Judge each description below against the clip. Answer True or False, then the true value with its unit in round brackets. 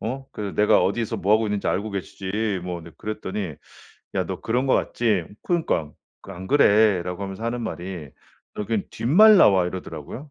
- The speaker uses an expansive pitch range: False (3.5 semitones)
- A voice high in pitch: False (105 Hz)